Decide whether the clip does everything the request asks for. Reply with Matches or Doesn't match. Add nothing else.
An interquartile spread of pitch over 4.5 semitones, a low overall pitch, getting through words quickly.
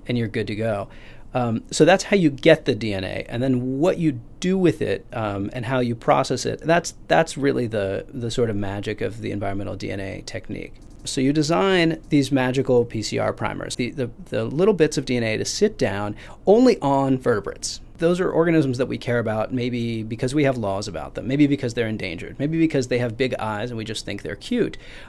Matches